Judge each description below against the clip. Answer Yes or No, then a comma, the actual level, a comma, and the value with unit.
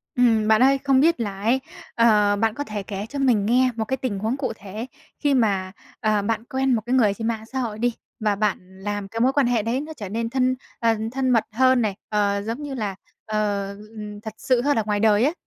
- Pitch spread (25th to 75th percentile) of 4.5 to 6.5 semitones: No, average, 3.7 semitones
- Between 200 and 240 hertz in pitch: Yes, high, 225 Hz